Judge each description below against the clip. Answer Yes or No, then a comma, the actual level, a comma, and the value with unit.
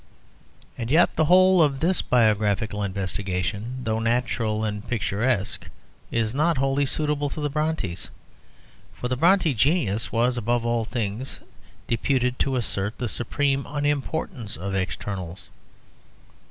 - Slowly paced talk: Yes, slow, 125 wpm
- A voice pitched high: No, low, 120 Hz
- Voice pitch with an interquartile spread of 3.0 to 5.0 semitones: No, wide, 5.5 semitones